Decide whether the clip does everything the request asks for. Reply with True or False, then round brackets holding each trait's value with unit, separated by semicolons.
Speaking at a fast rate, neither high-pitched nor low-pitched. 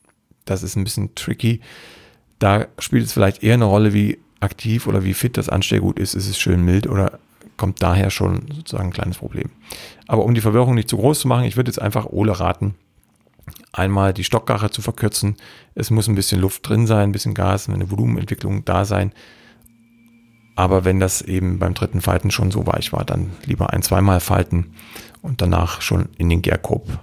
False (195 wpm; 105 Hz)